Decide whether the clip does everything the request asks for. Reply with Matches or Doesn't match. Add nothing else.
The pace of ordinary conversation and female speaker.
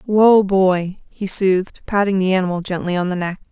Matches